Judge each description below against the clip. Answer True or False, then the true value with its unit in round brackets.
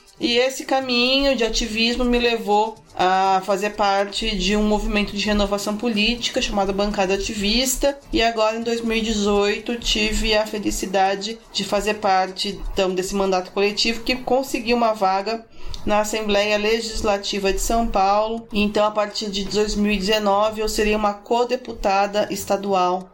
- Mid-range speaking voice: False (210 Hz)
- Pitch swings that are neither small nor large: False (2.3 semitones)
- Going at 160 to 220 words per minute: False (135 wpm)